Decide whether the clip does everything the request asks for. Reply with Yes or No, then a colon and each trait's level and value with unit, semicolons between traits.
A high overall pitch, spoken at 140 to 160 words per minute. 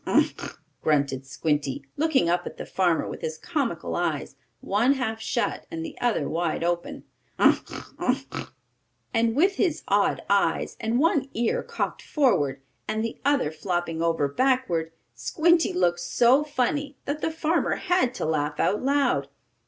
Yes: high, 225 Hz; average, 155 wpm